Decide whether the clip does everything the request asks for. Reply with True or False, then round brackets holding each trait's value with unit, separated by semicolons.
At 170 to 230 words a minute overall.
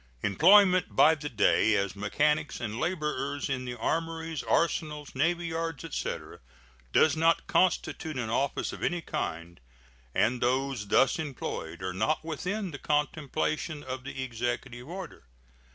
False (135 wpm)